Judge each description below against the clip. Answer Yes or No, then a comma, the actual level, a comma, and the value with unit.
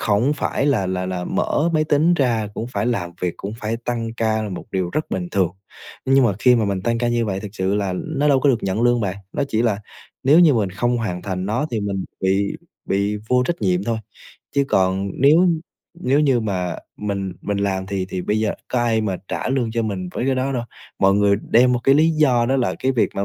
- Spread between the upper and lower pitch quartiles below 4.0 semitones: No, average, 4.6 semitones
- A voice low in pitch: Yes, low, 110 Hz